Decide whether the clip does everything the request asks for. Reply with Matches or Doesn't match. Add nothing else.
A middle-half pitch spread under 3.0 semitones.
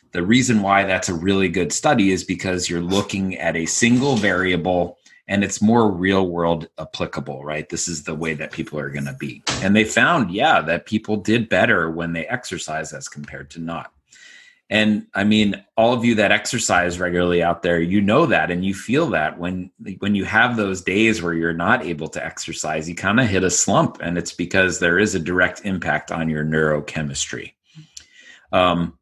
Doesn't match